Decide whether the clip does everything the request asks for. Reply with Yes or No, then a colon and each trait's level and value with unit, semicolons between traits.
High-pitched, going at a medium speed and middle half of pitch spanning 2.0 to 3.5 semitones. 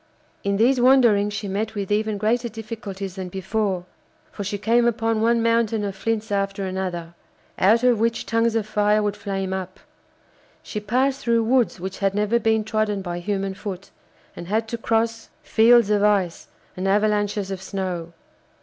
Yes: high, 210 Hz; average, 170 wpm; average, 2.7 semitones